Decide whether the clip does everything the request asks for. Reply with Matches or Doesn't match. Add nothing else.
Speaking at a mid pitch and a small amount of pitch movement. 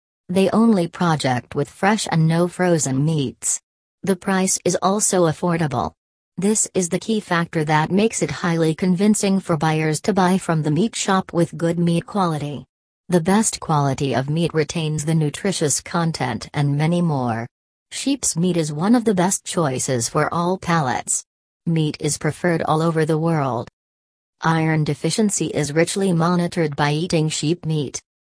Doesn't match